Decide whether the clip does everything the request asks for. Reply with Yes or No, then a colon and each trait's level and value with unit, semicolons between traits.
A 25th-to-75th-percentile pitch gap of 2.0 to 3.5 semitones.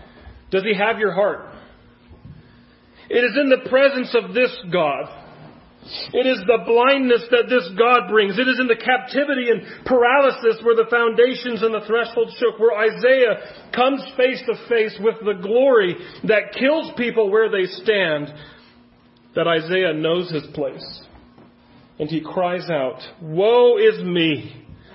No: average, 4.6 semitones